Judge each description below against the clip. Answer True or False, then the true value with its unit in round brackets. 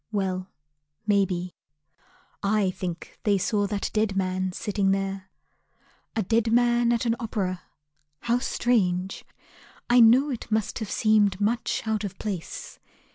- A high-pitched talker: True (205 Hz)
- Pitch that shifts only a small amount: False (3.2 semitones)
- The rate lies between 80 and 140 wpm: True (135 wpm)